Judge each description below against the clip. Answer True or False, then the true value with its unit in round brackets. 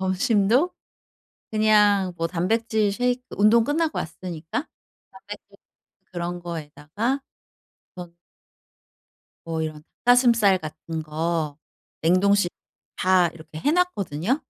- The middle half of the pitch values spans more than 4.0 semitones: True (5.3 semitones)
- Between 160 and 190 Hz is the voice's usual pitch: True (185 Hz)